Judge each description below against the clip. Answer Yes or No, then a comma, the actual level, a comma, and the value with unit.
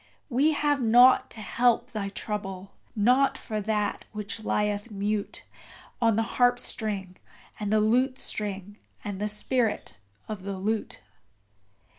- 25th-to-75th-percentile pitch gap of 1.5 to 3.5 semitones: Yes, average, 3.0 semitones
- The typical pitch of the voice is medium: No, high, 215 Hz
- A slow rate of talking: Yes, slow, 125 wpm